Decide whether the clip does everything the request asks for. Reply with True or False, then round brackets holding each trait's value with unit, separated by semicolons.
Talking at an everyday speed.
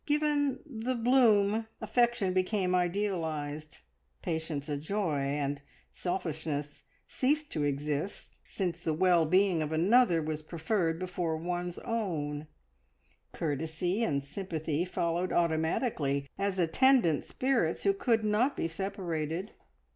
False (115 wpm)